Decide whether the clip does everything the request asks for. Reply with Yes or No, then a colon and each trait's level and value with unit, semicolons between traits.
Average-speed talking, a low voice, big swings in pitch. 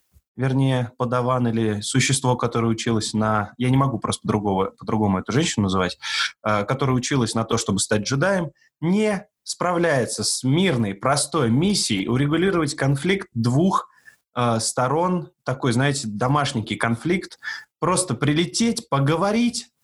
Yes: average, 125 wpm; low, 130 Hz; wide, 6.8 semitones